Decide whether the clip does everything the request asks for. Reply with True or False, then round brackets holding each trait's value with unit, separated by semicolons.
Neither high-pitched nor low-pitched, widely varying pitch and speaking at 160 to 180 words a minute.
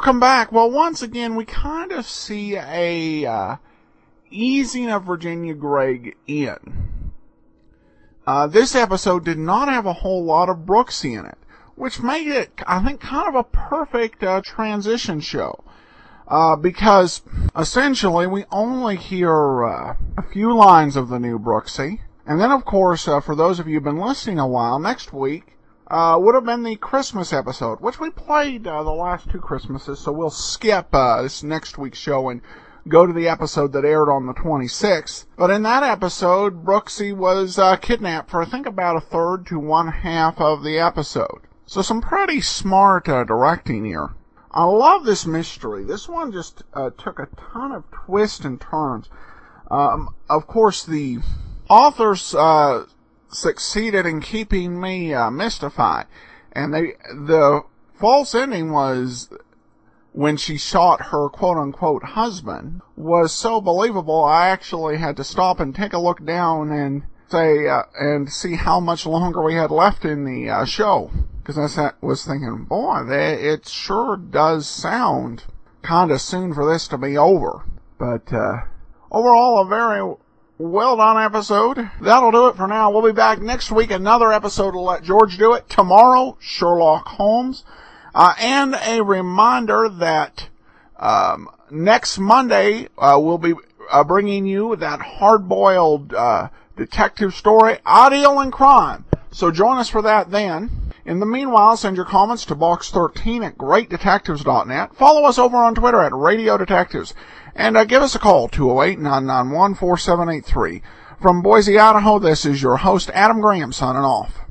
True (180 Hz; 6.4 semitones; 165 wpm)